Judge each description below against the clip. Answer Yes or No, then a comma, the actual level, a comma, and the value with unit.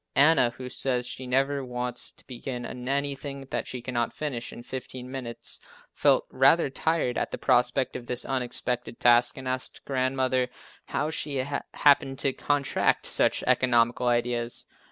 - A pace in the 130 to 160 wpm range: Yes, average, 150 wpm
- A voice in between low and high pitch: No, low, 130 Hz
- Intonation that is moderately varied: No, narrow, 1.8 semitones